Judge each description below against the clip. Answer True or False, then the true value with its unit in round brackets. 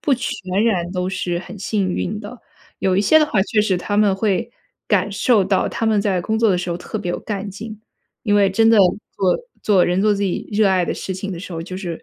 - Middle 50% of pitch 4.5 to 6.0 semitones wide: False (2.5 semitones)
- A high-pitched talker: True (200 Hz)